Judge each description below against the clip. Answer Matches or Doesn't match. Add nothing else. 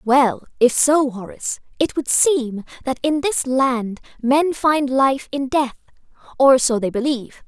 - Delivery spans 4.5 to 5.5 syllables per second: Doesn't match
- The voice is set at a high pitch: Matches